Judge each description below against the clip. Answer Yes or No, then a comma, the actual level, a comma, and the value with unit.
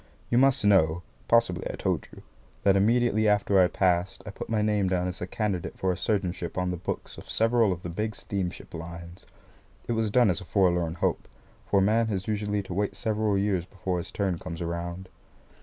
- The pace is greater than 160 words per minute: Yes, fast, 205 wpm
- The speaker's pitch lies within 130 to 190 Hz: No, very low, 95 Hz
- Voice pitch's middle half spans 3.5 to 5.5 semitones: No, average, 3.1 semitones